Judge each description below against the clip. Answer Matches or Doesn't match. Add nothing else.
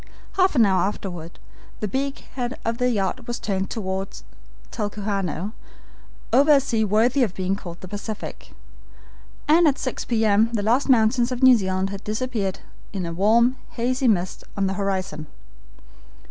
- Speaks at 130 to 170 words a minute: Matches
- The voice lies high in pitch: Matches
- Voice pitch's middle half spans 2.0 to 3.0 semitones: Doesn't match